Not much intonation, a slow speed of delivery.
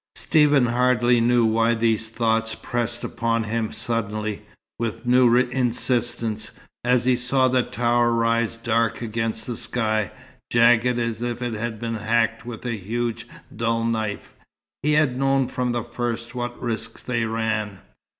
No: narrow, 1.4 semitones; average, 150 wpm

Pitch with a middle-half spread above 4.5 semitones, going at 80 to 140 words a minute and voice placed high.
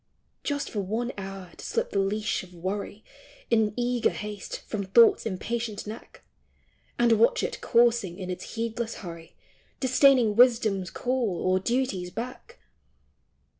No: average, 3.8 semitones; slow, 135 wpm; high, 220 Hz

